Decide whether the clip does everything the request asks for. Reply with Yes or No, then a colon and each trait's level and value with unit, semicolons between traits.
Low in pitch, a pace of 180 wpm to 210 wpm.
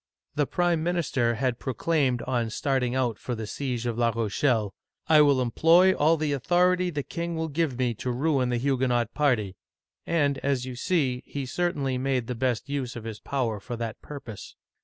Yes: low, 130 Hz; average, 200 wpm